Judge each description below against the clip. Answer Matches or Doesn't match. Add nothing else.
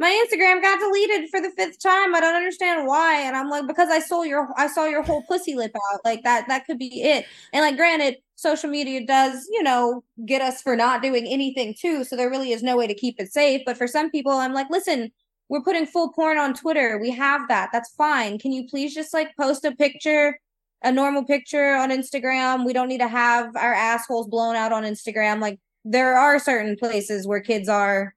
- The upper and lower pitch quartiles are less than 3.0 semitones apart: Doesn't match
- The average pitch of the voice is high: Matches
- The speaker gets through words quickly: Matches